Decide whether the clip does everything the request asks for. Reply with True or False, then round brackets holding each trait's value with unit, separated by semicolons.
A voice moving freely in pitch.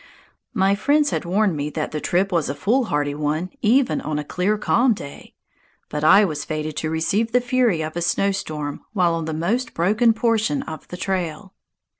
True (5.8 semitones)